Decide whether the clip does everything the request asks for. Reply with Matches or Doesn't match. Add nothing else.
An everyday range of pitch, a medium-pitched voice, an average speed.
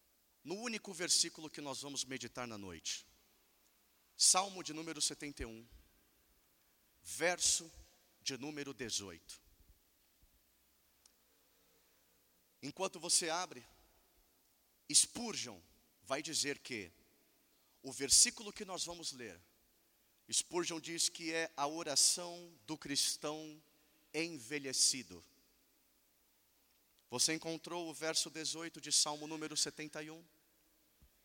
Doesn't match